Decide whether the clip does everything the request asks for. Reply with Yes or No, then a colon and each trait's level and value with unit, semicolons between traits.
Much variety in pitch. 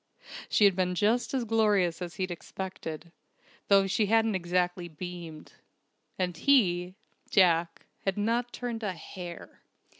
No: average, 3.4 semitones